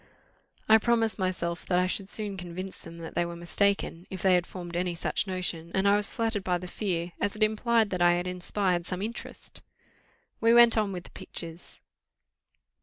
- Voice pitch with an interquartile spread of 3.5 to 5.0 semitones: No, average, 3.0 semitones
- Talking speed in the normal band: Yes, average, 190 wpm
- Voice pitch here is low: No, medium, 185 Hz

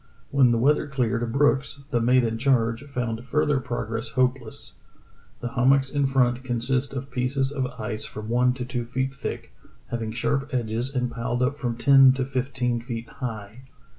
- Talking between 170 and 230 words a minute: Yes, average, 175 wpm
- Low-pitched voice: Yes, low, 125 Hz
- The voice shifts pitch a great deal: No, narrow, 2.4 semitones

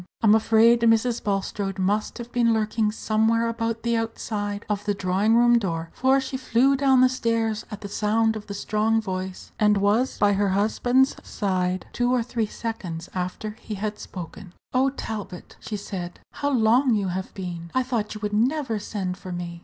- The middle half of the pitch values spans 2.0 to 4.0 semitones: Yes, average, 2.8 semitones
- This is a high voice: Yes, high, 215 Hz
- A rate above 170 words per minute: Yes, average, 185 wpm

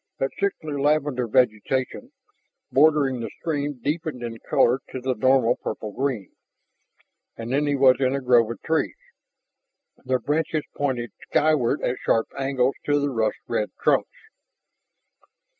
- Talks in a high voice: No, low, 130 Hz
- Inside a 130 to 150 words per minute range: Yes, average, 140 wpm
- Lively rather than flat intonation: No, average, 3.1 semitones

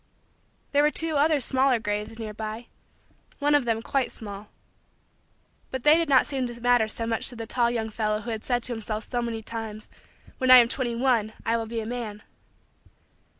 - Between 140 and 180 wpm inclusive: No, average, 195 wpm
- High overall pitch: Yes, high, 235 Hz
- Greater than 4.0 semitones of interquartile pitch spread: No, average, 2.7 semitones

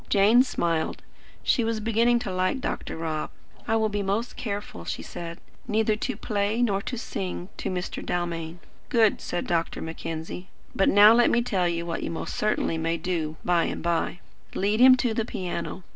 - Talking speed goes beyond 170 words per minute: Yes, average, 185 wpm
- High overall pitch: Yes, high, 195 Hz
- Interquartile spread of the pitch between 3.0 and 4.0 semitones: No, average, 4.6 semitones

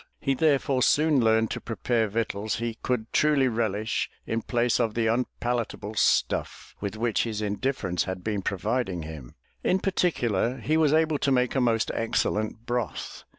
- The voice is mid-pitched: No, low, 115 Hz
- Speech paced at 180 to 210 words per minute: No, average, 160 wpm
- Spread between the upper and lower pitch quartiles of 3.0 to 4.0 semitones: Yes, average, 3.3 semitones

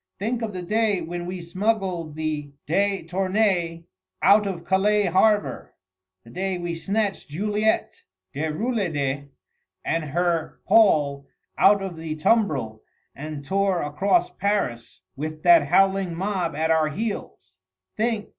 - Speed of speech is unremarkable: No, slow, 125 wpm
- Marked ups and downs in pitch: No, average, 4.5 semitones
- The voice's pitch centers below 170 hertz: No, medium, 180 Hz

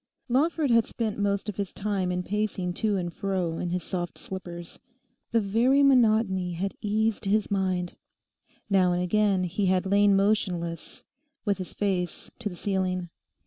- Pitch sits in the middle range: No, high, 195 Hz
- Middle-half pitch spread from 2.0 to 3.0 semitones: Yes, average, 2.7 semitones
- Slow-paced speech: No, average, 160 wpm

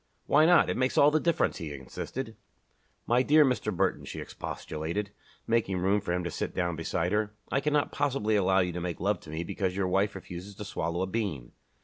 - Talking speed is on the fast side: Yes, fast, 215 wpm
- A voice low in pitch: Yes, low, 100 Hz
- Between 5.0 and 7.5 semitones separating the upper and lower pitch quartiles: Yes, average, 5.3 semitones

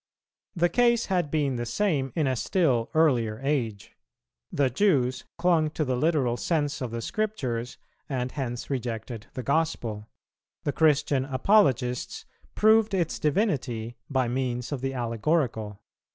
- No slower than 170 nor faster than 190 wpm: No, slow, 135 wpm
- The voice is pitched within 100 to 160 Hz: Yes, low, 135 Hz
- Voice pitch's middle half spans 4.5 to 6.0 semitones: Yes, average, 5.0 semitones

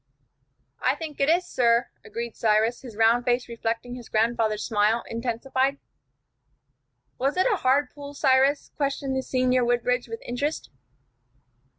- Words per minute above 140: No, slow, 135 wpm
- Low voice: No, high, 245 Hz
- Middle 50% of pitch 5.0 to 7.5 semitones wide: No, average, 2.9 semitones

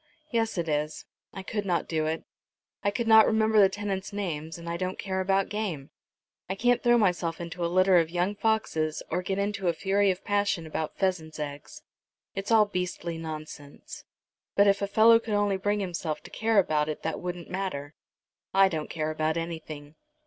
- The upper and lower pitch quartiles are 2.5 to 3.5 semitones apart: No, average, 4.1 semitones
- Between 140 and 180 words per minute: No, average, 190 wpm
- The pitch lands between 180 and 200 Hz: Yes, medium, 185 Hz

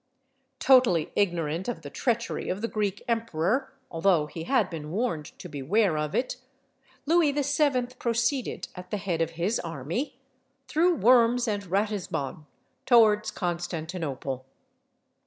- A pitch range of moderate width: No, wide, 6.8 semitones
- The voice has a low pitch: No, high, 200 Hz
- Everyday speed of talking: No, slow, 130 wpm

